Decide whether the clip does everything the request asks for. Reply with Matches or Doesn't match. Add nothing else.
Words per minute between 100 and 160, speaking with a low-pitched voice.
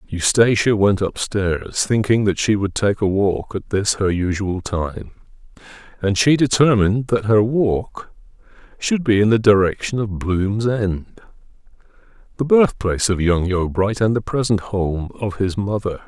Matches